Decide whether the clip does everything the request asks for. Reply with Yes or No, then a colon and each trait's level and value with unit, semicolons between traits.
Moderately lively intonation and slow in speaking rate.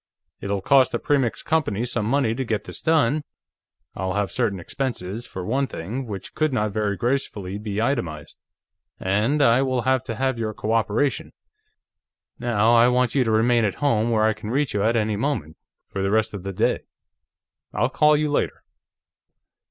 No: average, 4.3 semitones; average, 180 wpm